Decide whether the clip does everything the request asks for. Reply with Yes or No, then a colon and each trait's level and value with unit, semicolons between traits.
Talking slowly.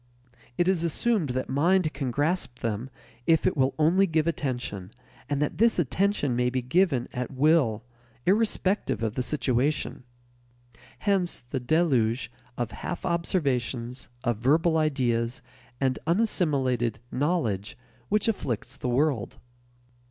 Yes: slow, 130 wpm